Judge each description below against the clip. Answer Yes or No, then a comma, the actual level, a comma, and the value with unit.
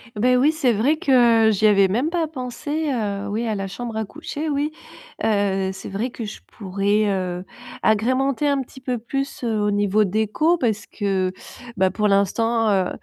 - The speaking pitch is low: No, high, 220 Hz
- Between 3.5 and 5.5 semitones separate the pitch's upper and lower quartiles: Yes, average, 4.4 semitones